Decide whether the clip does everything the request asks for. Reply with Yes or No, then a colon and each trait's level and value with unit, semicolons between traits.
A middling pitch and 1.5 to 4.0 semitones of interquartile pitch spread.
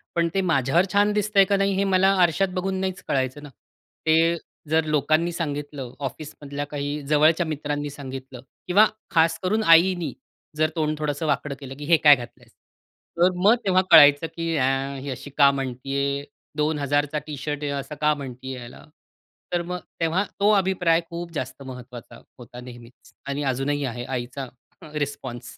Yes: medium, 150 Hz; average, 3.6 semitones